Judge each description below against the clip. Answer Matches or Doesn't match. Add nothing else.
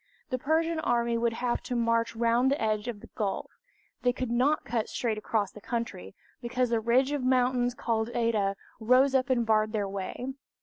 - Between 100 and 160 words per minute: Doesn't match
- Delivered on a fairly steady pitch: Matches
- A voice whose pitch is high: Matches